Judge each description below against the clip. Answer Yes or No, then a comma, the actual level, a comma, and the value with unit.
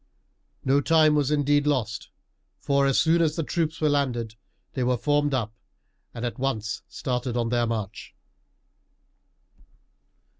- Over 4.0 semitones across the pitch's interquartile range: No, average, 3.7 semitones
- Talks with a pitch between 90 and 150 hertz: Yes, low, 135 Hz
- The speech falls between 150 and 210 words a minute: No, average, 140 wpm